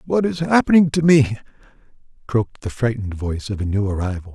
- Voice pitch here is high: No, low, 125 Hz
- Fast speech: No, average, 180 wpm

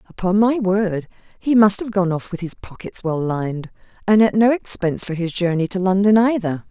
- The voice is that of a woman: Yes, female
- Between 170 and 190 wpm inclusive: No, fast, 205 wpm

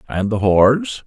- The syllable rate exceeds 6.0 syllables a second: No, 4.5 syllables/s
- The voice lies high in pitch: No, low, 115 Hz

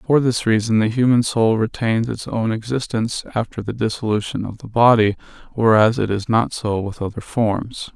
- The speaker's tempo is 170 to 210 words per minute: Yes, average, 180 wpm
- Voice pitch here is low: Yes, low, 115 Hz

